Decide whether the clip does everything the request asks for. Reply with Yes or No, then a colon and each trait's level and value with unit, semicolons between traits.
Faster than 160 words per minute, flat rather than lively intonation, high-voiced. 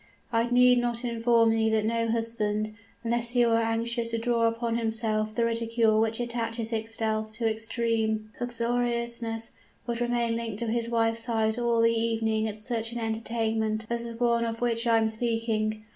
Yes: average, 175 wpm; narrow, 1.1 semitones; high, 230 Hz